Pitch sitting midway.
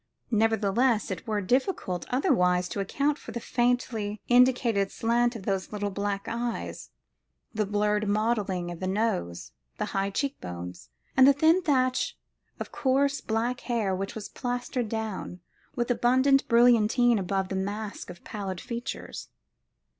No: high, 220 Hz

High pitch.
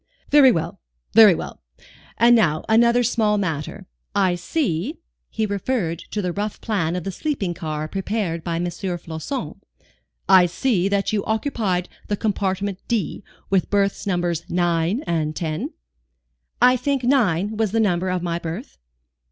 Yes: high, 195 Hz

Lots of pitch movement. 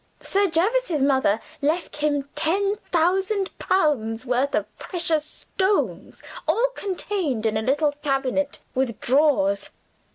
Yes: wide, 6.0 semitones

